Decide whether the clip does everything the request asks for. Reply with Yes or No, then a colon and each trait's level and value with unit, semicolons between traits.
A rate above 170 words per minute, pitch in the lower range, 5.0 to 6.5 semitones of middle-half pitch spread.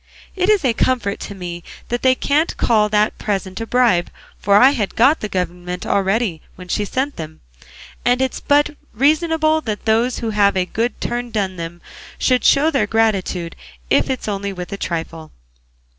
No: average, 185 wpm; high, 215 Hz; wide, 5.4 semitones